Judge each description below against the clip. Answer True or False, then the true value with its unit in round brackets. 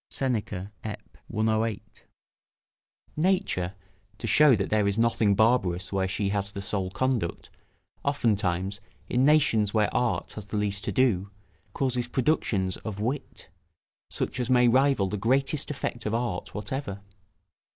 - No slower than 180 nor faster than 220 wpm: False (140 wpm)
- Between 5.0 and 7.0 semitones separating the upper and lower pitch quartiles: False (4.2 semitones)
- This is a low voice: True (110 Hz)